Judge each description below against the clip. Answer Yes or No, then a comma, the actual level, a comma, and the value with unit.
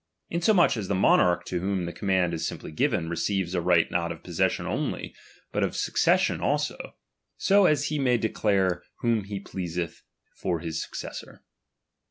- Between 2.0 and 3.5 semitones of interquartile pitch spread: No, average, 4.3 semitones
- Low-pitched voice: Yes, very low, 95 Hz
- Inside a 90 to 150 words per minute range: No, average, 165 wpm